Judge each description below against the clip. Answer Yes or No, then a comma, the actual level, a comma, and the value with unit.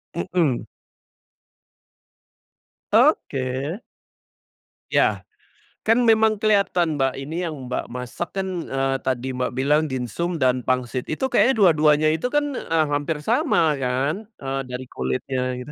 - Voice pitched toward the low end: No, medium, 145 Hz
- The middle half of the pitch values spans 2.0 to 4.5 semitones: No, average, 5.3 semitones